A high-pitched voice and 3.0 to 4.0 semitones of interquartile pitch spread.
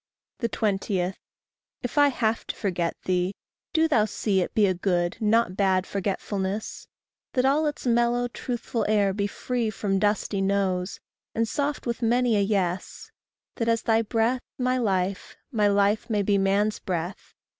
Yes: high, 210 Hz; average, 3.4 semitones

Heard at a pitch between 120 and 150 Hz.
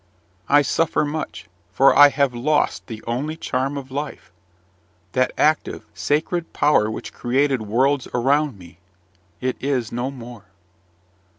Yes: low, 135 Hz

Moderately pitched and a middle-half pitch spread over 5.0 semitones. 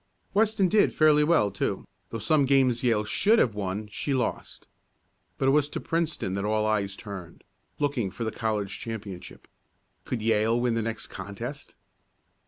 No: low, 115 Hz; wide, 5.5 semitones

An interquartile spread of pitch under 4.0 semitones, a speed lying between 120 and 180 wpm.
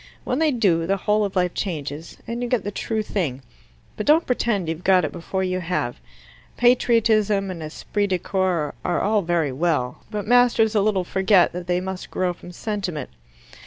No: average, 3.6 semitones; average, 190 wpm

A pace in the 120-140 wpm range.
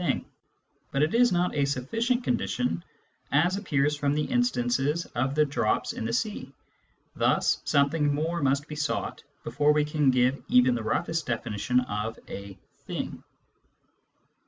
No: average, 160 wpm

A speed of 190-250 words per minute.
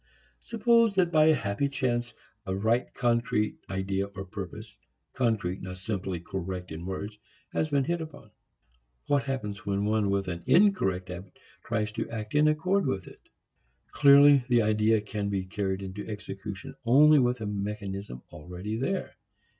No: average, 155 wpm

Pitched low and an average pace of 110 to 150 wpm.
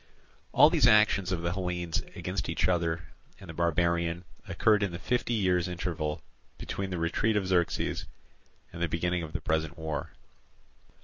No: very low, 85 Hz; average, 165 wpm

